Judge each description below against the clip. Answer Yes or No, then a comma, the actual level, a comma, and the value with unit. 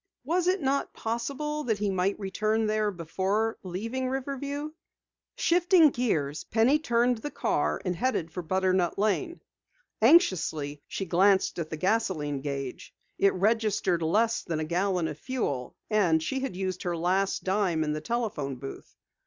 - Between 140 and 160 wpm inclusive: Yes, average, 155 wpm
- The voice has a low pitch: No, high, 200 Hz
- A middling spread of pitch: No, wide, 6.3 semitones